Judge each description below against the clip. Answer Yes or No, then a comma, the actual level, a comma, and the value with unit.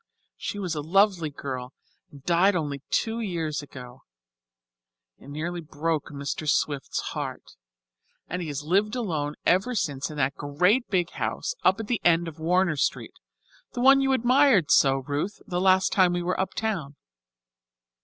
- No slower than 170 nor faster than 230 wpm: No, average, 160 wpm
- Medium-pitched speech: Yes, medium, 170 Hz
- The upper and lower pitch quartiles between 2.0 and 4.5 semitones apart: No, average, 5.1 semitones